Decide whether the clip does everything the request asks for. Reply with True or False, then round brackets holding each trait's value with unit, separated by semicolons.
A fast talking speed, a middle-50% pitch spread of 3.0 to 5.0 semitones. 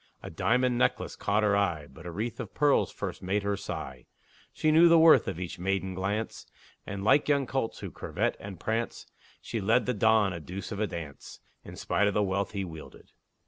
True (210 wpm; 3.6 semitones)